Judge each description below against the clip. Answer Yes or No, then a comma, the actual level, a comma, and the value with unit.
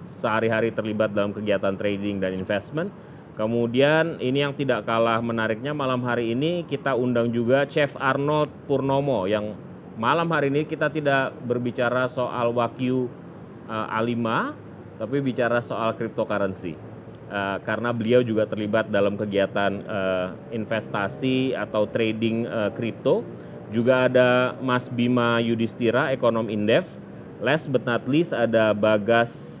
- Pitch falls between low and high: No, low, 115 Hz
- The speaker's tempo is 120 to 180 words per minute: Yes, average, 130 wpm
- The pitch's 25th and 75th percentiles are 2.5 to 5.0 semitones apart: Yes, average, 3.4 semitones